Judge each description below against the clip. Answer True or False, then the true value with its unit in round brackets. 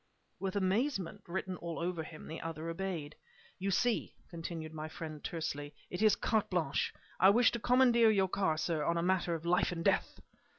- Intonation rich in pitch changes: False (3.4 semitones)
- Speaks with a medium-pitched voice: True (175 Hz)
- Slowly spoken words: False (185 wpm)